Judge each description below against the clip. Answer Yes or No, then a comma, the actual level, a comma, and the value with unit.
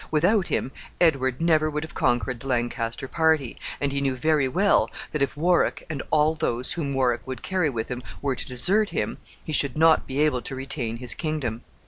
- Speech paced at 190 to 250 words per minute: Yes, average, 200 wpm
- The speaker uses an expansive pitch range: No, average, 3.9 semitones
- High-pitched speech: No, medium, 140 Hz